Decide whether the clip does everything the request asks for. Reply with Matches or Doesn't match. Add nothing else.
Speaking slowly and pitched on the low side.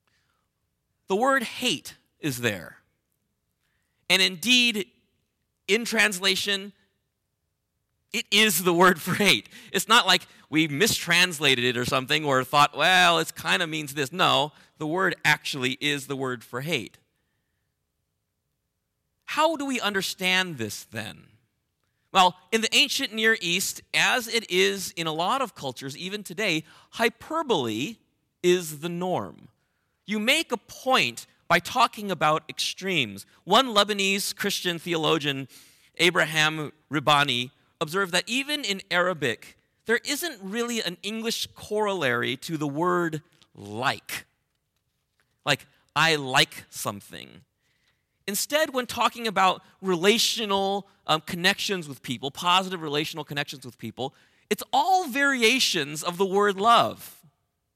Doesn't match